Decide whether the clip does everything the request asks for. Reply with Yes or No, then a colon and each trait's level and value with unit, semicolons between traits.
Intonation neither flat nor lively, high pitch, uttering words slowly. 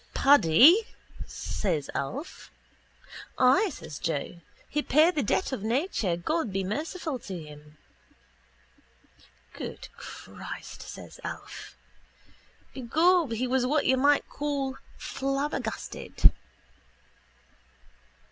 No: wide, 7.5 semitones; very high, 265 Hz; slow, 95 wpm